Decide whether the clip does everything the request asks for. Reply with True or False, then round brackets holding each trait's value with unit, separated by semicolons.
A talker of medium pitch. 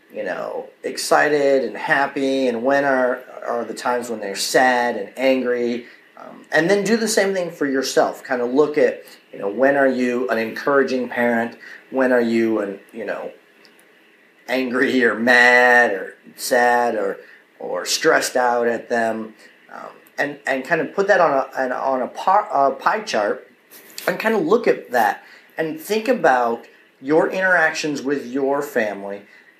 False (130 Hz)